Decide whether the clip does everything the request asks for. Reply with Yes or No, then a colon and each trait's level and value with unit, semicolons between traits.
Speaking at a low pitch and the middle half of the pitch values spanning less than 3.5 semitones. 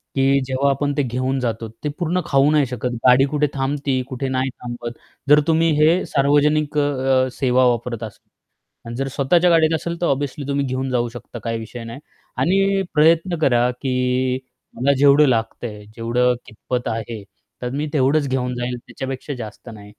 Yes: low, 130 Hz; average, 2.9 semitones